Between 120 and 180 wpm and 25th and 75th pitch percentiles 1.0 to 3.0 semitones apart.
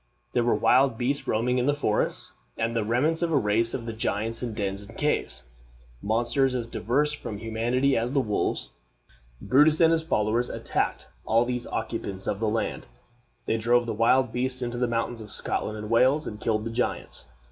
No: average, 190 wpm; narrow, 2.5 semitones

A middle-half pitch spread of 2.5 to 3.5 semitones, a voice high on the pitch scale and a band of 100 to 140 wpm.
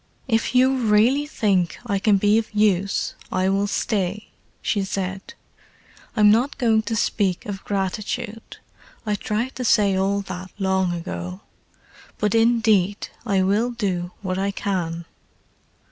Yes: average, 2.8 semitones; high, 205 Hz; slow, 135 wpm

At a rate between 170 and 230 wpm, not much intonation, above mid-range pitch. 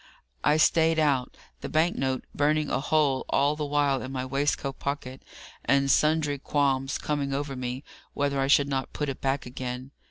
No: average, 180 wpm; narrow, 1.8 semitones; medium, 140 Hz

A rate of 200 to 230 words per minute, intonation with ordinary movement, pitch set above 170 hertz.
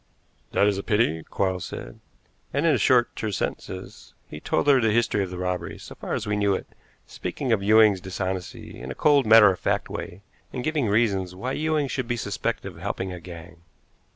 No: fast, 205 wpm; average, 4.5 semitones; low, 100 Hz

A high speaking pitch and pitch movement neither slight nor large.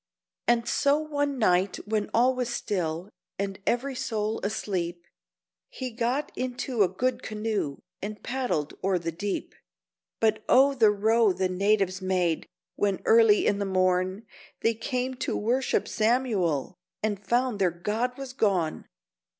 Yes: high, 215 Hz; average, 4.6 semitones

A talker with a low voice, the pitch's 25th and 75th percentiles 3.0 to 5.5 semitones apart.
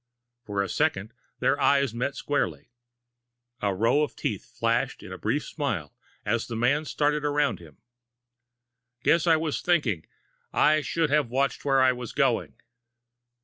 Yes: low, 130 Hz; average, 4.9 semitones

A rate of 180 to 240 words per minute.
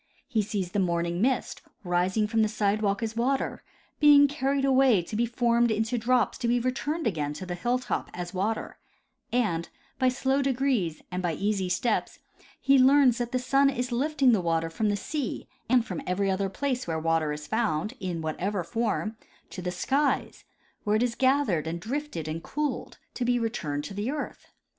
Yes: average, 190 wpm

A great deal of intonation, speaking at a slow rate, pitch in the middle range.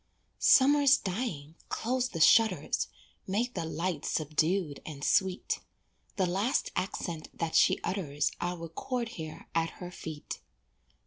Yes: wide, 5.8 semitones; slow, 125 wpm; medium, 180 Hz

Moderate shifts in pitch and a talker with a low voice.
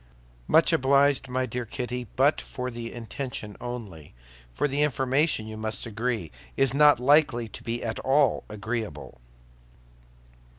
Yes: average, 3.5 semitones; low, 120 Hz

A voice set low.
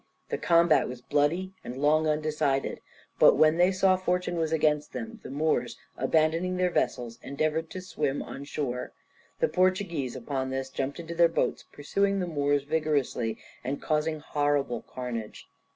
No: medium, 150 Hz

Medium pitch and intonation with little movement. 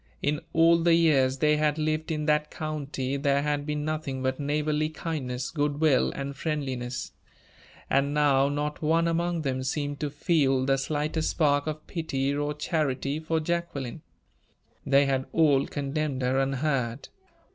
Yes: medium, 145 Hz; narrow, 2.2 semitones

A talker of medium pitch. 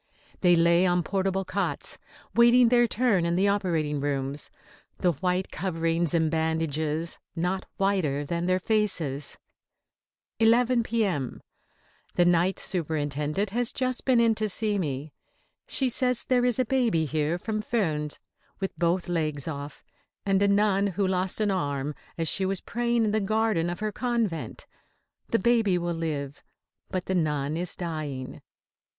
Yes: medium, 180 Hz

